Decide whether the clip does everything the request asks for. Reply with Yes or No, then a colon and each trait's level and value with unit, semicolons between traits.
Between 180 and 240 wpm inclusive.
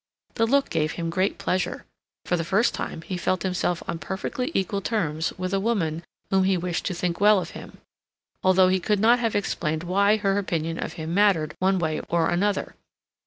Yes: average, 200 wpm